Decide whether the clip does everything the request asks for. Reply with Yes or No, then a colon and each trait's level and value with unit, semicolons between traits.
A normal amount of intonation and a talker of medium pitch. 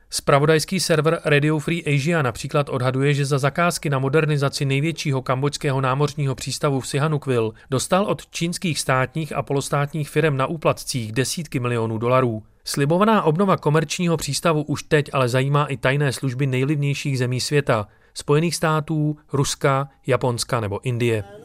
Yes: average, 3.0 semitones; medium, 145 Hz